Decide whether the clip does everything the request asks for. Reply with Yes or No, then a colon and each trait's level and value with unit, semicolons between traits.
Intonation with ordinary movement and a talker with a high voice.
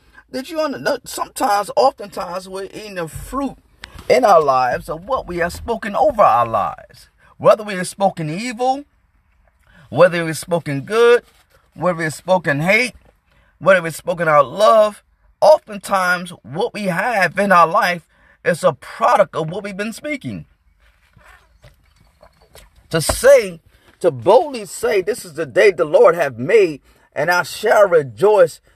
No: wide, 6.8 semitones; high, 205 Hz